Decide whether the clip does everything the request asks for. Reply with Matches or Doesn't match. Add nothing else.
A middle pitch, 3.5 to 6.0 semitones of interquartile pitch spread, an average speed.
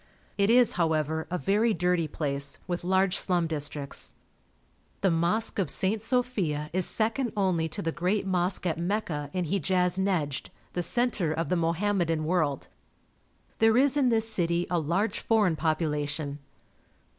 Matches